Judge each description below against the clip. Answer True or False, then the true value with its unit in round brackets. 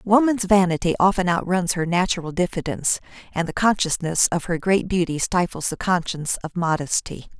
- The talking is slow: False (155 wpm)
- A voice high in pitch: False (175 Hz)